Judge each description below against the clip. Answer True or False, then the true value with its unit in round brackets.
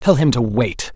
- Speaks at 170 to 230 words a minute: False (250 wpm)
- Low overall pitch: True (125 Hz)